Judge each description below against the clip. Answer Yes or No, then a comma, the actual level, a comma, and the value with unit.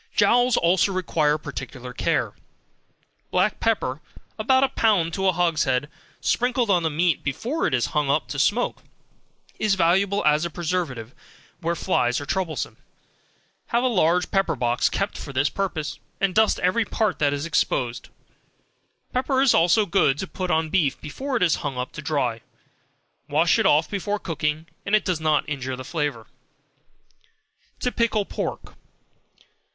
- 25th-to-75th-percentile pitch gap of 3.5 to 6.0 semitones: Yes, wide, 5.5 semitones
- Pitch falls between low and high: Yes, medium, 170 Hz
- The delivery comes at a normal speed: Yes, average, 160 wpm